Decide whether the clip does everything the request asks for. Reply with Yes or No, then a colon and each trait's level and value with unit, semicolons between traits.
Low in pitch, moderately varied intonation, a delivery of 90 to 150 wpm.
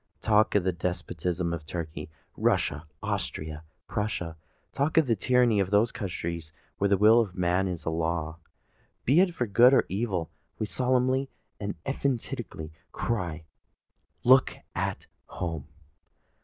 No: very low, 95 Hz; wide, 6.2 semitones; average, 140 wpm